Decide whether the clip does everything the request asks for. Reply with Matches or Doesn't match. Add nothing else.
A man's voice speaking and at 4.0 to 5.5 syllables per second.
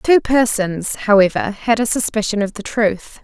Doesn't match